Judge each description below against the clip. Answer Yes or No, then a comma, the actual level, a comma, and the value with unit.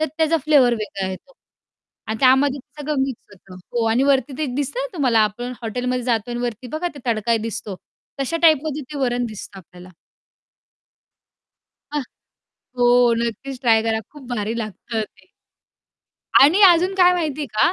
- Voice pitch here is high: Yes, very high, 250 Hz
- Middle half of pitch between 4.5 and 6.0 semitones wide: Yes, average, 4.8 semitones